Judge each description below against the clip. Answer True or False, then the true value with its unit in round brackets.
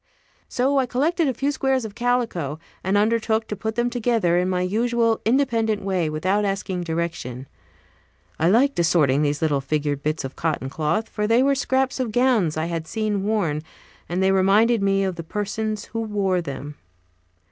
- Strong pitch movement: True (5.7 semitones)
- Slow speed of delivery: False (180 wpm)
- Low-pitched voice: False (205 Hz)